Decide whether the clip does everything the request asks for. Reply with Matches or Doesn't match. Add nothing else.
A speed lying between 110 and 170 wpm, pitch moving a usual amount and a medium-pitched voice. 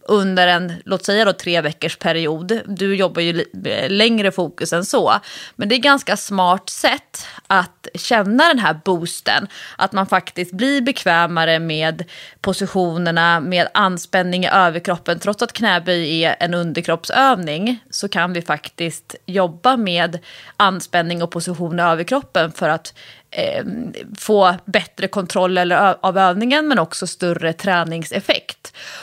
Matches